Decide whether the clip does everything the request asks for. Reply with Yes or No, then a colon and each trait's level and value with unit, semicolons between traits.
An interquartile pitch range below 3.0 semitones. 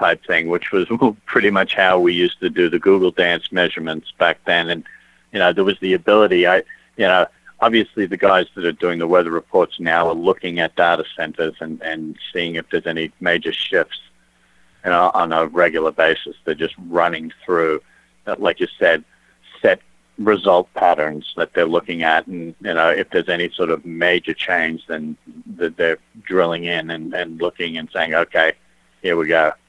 Yes: narrow, 2.6 semitones